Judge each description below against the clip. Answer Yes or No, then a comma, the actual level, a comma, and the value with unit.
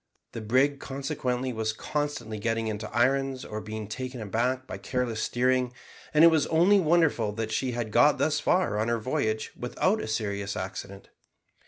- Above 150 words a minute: Yes, average, 170 wpm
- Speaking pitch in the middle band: No, low, 120 Hz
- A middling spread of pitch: Yes, average, 3.7 semitones